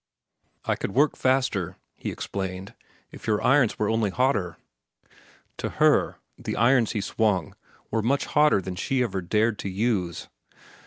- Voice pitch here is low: Yes, low, 110 Hz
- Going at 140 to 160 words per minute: Yes, average, 150 wpm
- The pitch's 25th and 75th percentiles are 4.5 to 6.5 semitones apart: Yes, average, 4.8 semitones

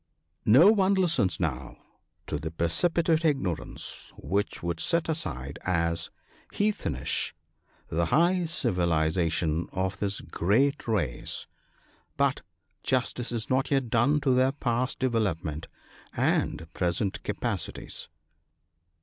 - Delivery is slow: Yes, slow, 120 wpm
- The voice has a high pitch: No, low, 105 Hz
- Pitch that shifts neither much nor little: No, wide, 8.9 semitones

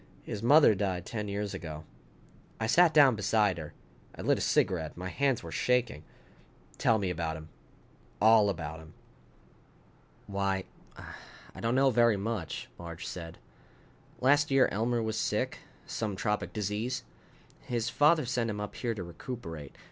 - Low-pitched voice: Yes, low, 105 Hz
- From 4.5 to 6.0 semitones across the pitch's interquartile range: Yes, average, 5.1 semitones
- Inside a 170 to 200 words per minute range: No, average, 150 wpm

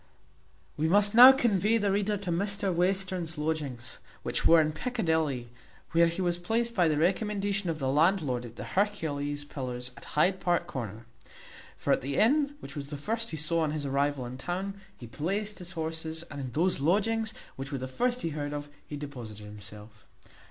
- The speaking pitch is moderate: Yes, medium, 160 Hz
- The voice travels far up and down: Yes, wide, 5.9 semitones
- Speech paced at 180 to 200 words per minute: Yes, average, 190 wpm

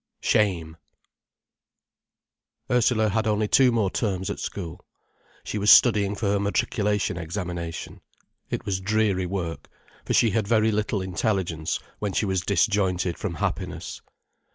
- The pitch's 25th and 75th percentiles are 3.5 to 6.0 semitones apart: No, average, 2.8 semitones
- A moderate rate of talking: No, slow, 130 wpm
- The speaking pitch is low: Yes, low, 100 Hz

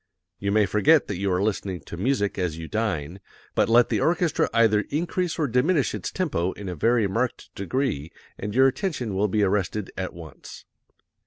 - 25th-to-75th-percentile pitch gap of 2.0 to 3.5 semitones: No, average, 5.2 semitones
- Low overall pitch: Yes, low, 105 Hz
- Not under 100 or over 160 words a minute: No, average, 185 wpm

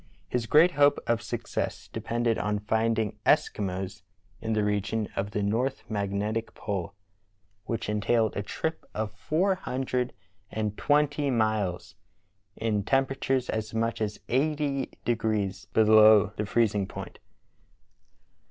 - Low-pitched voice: Yes, low, 110 Hz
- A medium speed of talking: No, slow, 125 wpm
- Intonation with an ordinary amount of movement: Yes, average, 3.2 semitones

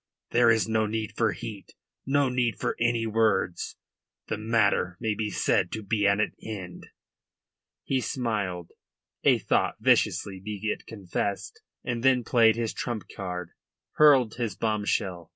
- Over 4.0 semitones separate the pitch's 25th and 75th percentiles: No, average, 2.8 semitones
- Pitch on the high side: No, low, 110 Hz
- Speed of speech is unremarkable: Yes, average, 150 wpm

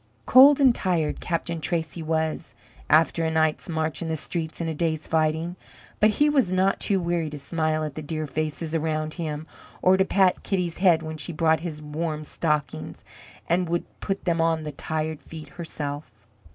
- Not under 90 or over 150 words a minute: No, average, 185 wpm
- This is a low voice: No, medium, 160 Hz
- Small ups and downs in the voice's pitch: Yes, narrow, 1.9 semitones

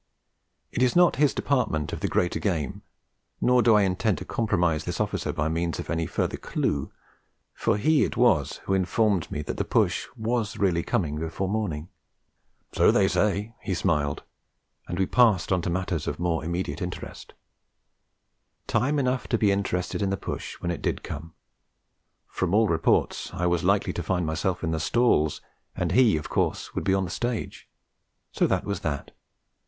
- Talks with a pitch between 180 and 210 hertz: No, very low, 95 Hz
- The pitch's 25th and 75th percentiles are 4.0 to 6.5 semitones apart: Yes, average, 4.9 semitones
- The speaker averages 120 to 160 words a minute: No, average, 180 wpm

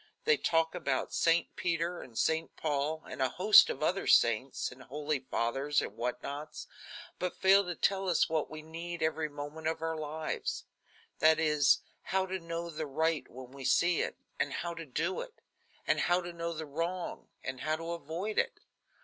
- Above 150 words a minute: Yes, average, 190 wpm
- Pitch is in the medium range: Yes, medium, 160 Hz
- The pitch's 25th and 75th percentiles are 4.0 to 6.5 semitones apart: No, average, 2.8 semitones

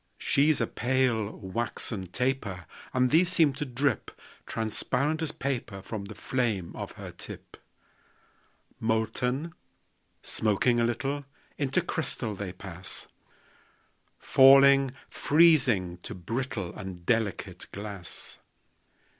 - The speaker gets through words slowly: Yes, slow, 105 wpm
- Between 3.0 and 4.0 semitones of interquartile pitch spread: No, average, 5.3 semitones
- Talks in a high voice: No, low, 120 Hz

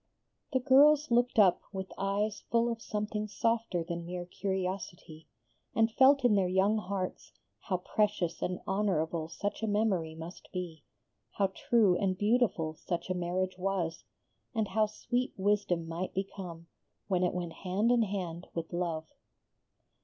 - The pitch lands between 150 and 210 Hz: Yes, high, 190 Hz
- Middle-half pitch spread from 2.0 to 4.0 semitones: Yes, average, 3.4 semitones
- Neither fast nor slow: Yes, average, 150 wpm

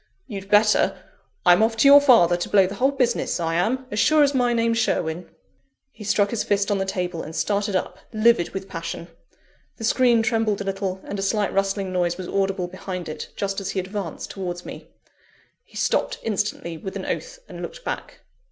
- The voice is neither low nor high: No, high, 200 Hz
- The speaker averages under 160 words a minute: No, average, 200 wpm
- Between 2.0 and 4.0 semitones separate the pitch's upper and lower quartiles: Yes, average, 3.6 semitones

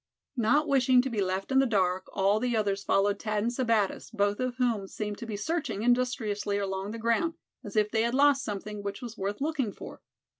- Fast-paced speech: Yes, fast, 215 wpm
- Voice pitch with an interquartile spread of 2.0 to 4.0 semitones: Yes, average, 3.7 semitones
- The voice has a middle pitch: No, high, 220 Hz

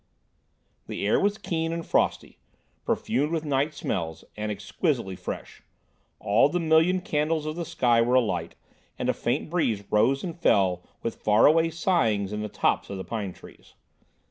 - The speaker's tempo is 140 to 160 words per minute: No, average, 170 wpm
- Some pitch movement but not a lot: No, wide, 7.7 semitones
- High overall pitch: No, low, 130 Hz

